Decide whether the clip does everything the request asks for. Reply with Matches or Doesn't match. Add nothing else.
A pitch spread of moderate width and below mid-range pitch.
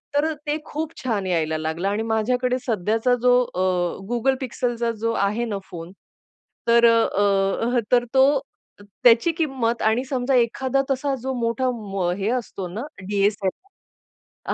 Doesn't match